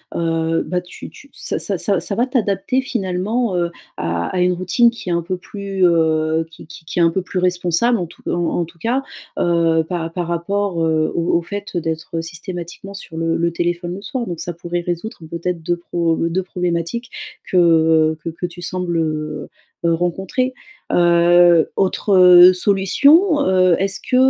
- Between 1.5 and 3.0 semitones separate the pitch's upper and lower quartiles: Yes, narrow, 2.5 semitones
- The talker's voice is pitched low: No, medium, 175 Hz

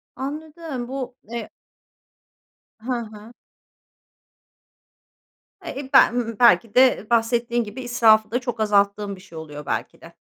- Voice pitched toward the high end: Yes, high, 235 Hz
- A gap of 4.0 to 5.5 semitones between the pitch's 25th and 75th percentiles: No, average, 3.2 semitones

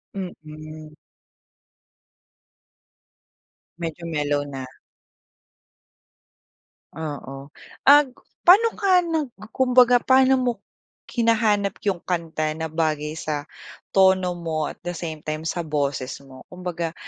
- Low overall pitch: No, medium, 165 Hz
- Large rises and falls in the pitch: Yes, wide, 6.8 semitones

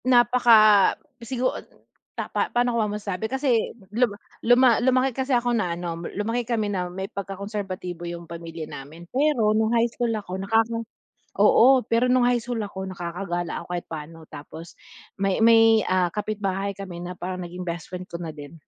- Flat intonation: No, average, 4.8 semitones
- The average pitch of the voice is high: Yes, high, 200 Hz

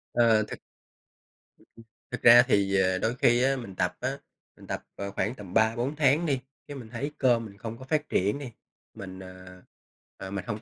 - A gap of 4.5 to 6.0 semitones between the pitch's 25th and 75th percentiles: Yes, average, 5.1 semitones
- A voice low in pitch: Yes, low, 115 Hz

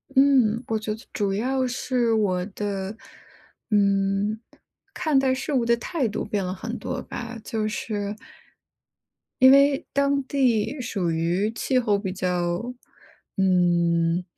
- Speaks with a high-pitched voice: Yes, high, 215 Hz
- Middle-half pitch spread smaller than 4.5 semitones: No, average, 4.8 semitones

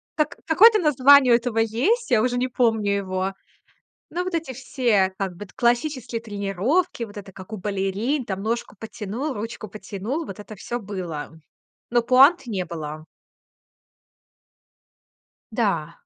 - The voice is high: Yes, high, 225 Hz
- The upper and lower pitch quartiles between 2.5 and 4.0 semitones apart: No, average, 4.8 semitones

